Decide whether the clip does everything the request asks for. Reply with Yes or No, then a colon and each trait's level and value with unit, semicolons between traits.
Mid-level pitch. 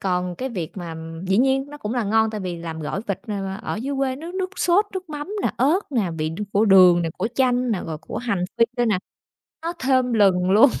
No: high, 220 Hz